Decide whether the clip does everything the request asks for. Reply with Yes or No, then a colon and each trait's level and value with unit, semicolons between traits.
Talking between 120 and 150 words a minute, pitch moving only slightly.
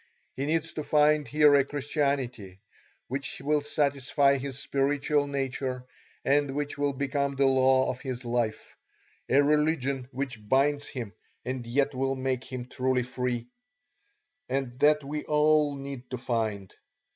Yes: average, 145 wpm; narrow, 2.1 semitones